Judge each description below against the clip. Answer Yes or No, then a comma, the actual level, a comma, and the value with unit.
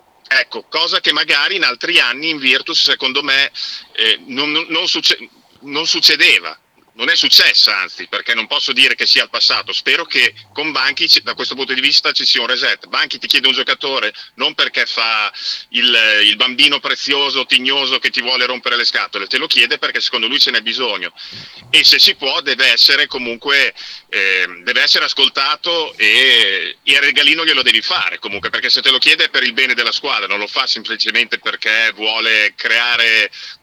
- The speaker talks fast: Yes, fast, 185 wpm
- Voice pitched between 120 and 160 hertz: Yes, medium, 140 Hz